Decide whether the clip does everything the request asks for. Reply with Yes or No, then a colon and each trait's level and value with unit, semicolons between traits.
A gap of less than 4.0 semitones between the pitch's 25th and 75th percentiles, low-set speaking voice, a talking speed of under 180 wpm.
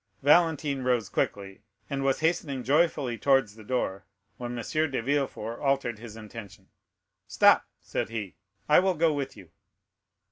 No: average, 4.5 semitones; low, 130 Hz; average, 145 wpm